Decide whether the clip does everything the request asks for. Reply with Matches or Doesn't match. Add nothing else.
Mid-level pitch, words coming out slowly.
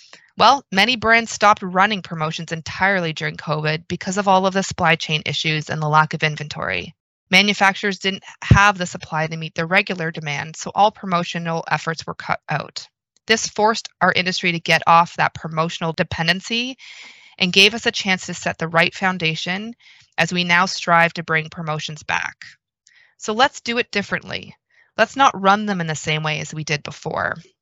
Doesn't match